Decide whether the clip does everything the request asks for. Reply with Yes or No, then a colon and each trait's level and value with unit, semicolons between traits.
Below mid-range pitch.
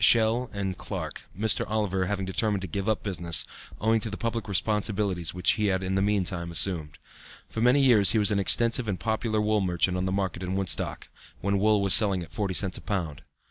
Yes: low, 100 Hz